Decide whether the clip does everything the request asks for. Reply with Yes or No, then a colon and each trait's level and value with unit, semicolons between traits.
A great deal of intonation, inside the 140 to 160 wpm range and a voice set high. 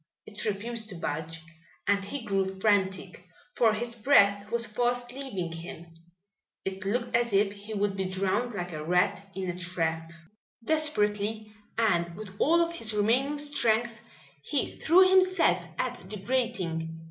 No: average, 4.3 semitones; average, 150 wpm; high, 210 Hz